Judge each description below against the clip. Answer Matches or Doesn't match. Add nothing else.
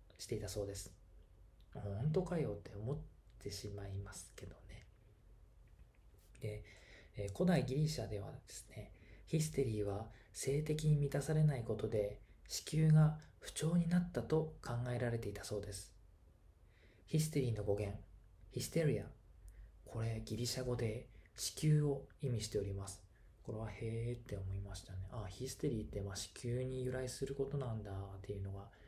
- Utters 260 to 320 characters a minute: Matches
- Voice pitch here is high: Doesn't match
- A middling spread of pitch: Matches